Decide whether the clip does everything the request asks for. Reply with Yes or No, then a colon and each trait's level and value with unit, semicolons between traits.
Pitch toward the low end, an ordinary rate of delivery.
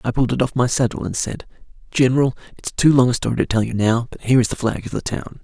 No: low, 120 Hz; fast, 285 wpm